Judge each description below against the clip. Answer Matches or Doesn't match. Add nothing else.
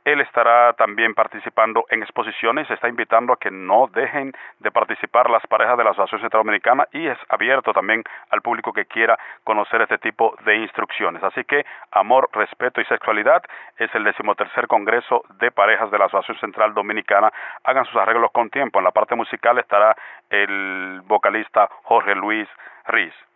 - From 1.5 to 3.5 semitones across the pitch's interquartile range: Matches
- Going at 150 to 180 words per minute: Matches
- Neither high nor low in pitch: Doesn't match